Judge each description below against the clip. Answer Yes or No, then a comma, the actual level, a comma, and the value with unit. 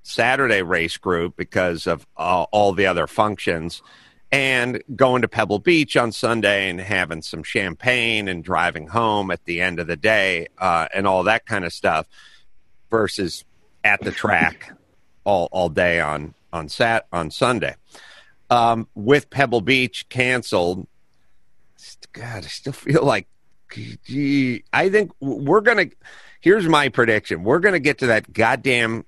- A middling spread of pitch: No, wide, 5.9 semitones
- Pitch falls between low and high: No, low, 110 Hz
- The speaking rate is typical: Yes, average, 155 wpm